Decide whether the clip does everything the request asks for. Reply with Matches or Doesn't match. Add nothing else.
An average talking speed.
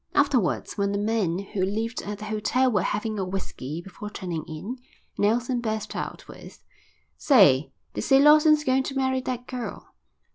Matches